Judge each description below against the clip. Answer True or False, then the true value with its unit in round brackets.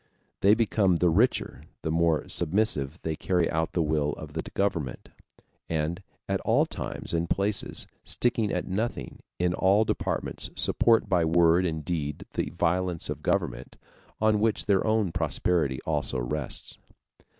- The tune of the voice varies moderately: True (4.0 semitones)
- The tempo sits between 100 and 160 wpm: True (150 wpm)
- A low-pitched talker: True (85 Hz)